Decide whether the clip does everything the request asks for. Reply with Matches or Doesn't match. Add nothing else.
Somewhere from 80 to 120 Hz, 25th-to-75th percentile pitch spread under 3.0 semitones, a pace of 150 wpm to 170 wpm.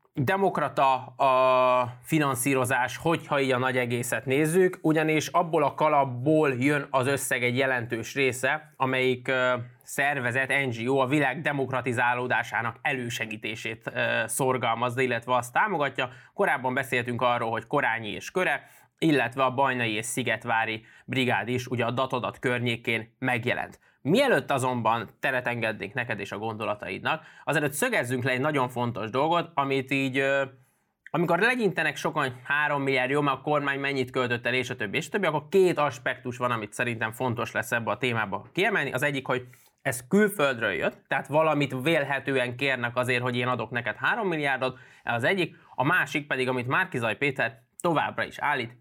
Doesn't match